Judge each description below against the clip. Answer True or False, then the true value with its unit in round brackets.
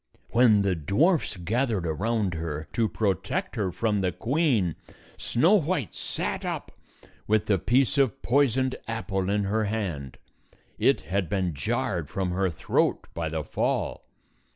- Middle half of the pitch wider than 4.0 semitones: True (4.9 semitones)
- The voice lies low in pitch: True (105 Hz)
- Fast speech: False (150 wpm)